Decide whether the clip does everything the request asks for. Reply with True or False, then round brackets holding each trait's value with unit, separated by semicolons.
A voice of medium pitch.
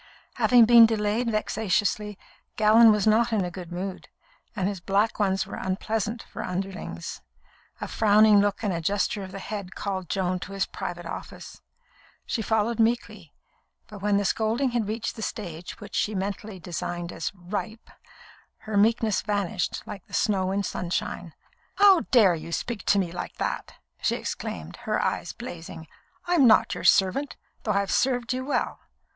False (205 Hz)